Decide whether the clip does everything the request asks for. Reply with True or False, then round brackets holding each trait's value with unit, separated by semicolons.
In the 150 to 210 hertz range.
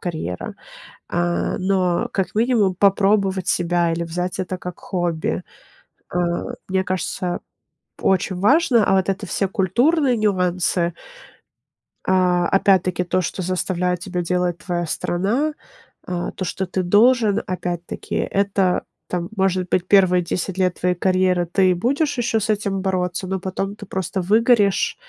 True (185 Hz)